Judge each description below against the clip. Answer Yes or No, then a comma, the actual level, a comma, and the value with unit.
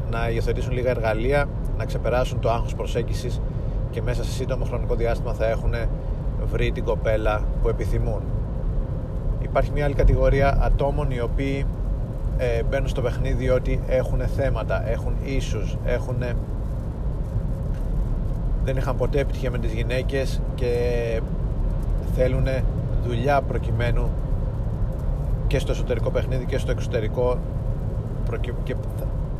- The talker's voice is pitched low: Yes, low, 125 Hz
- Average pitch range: No, narrow, 2.3 semitones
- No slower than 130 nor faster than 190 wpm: No, slow, 115 wpm